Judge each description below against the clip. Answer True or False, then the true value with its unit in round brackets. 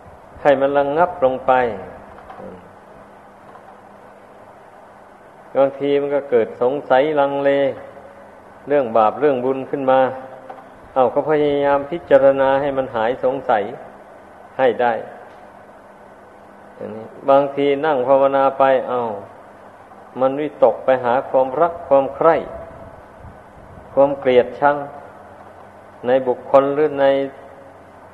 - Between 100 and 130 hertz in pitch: False (140 Hz)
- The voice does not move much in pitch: True (1.5 semitones)